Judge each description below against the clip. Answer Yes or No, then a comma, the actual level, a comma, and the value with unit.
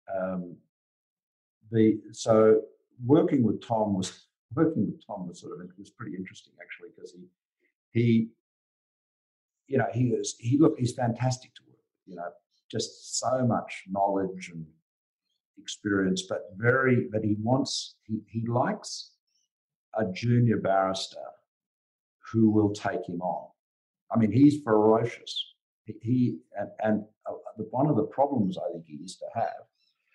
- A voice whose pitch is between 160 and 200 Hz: No, low, 110 Hz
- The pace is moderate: Yes, average, 150 wpm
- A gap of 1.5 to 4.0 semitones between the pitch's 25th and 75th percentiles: Yes, average, 3.7 semitones